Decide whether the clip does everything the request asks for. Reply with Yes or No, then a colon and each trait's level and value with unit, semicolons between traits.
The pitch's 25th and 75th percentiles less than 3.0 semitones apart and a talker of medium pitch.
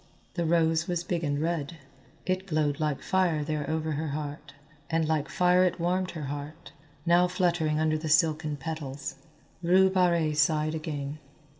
Yes: narrow, 2.4 semitones; medium, 160 Hz